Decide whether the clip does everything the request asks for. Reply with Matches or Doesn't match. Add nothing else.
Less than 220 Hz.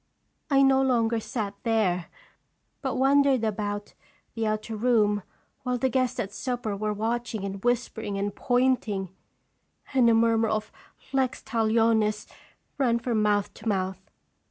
Doesn't match